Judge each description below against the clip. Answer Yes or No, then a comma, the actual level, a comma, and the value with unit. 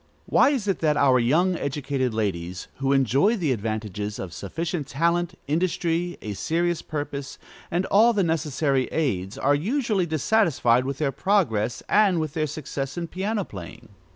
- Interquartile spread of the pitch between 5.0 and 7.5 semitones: Yes, wide, 5.5 semitones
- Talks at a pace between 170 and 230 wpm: No, average, 160 wpm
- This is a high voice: No, medium, 150 Hz